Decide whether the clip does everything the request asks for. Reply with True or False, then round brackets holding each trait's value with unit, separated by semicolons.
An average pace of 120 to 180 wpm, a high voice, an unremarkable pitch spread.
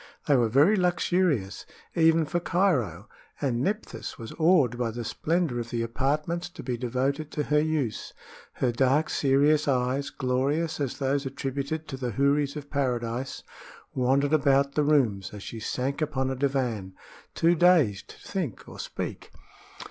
False (155 wpm; 140 Hz; 3.8 semitones)